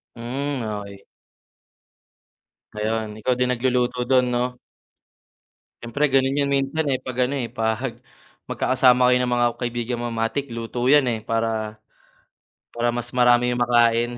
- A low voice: Yes, low, 120 Hz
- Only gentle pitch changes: Yes, narrow, 1.9 semitones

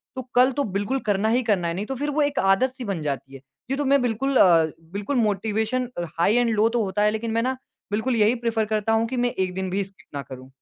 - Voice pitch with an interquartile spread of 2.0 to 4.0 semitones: No, average, 4.4 semitones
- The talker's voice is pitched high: Yes, high, 220 Hz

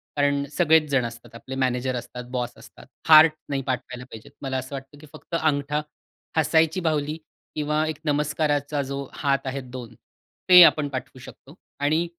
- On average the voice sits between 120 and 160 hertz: Yes, medium, 140 Hz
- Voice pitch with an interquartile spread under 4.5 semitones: Yes, average, 2.8 semitones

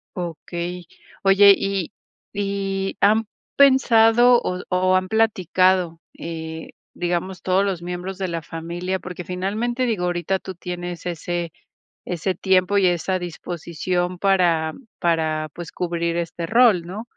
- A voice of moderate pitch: Yes, medium, 180 Hz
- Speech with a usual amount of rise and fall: No, narrow, 2.2 semitones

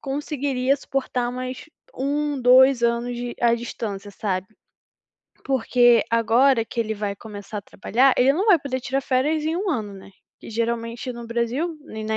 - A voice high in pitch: Yes, high, 245 Hz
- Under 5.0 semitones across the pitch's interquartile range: Yes, average, 3.1 semitones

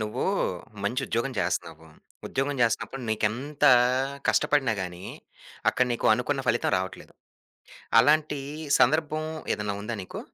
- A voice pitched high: No, low, 120 Hz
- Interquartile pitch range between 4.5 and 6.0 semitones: Yes, wide, 5.4 semitones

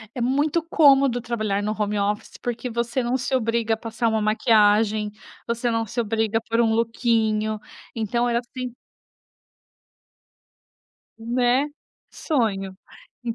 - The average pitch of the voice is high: Yes, high, 230 Hz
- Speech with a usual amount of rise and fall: No, narrow, 2.1 semitones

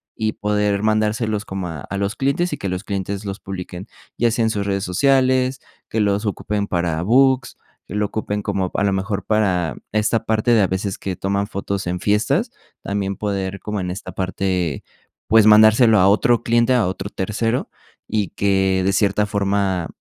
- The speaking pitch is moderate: No, low, 100 Hz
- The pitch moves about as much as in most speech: No, narrow, 2.1 semitones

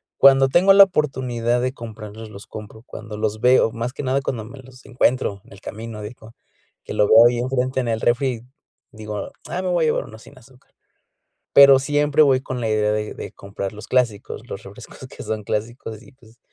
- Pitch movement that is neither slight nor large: Yes, average, 3.5 semitones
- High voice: No, low, 120 Hz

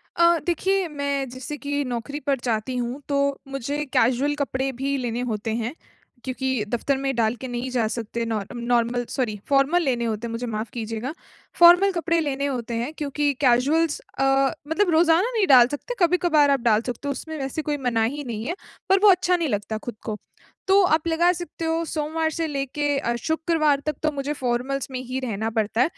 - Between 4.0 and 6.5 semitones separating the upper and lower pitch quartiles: Yes, average, 4.6 semitones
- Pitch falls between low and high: No, very high, 275 Hz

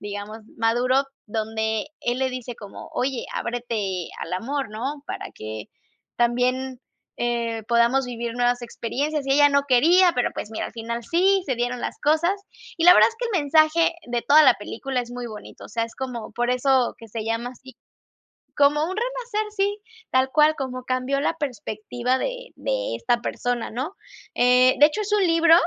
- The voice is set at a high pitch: Yes, very high, 255 Hz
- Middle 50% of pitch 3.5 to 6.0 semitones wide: Yes, average, 4.4 semitones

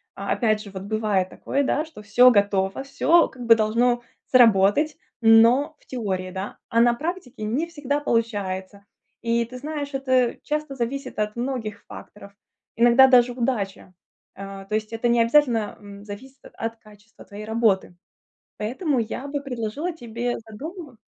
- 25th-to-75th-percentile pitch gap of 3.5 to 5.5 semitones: Yes, average, 4.1 semitones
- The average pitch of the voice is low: No, high, 235 Hz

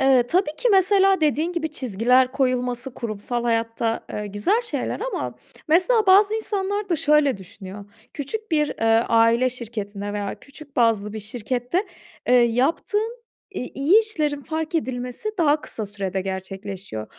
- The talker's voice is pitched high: Yes, very high, 255 Hz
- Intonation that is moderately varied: No, wide, 7.3 semitones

